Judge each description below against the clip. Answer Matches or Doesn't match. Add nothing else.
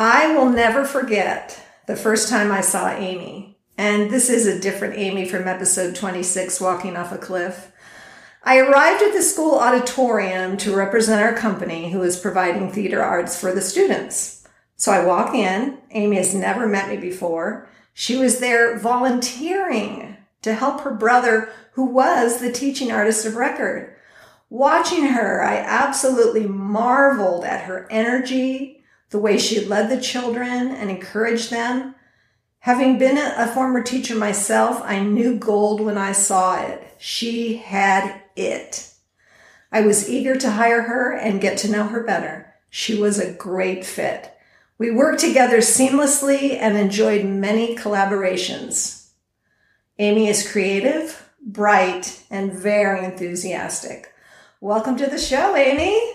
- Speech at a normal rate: Matches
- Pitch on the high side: Matches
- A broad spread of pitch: Doesn't match